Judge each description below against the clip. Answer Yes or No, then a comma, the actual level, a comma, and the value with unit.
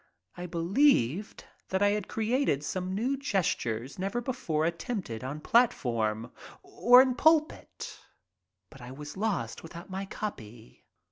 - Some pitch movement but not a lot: No, wide, 8.9 semitones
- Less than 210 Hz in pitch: Yes, medium, 185 Hz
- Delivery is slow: Yes, slow, 130 wpm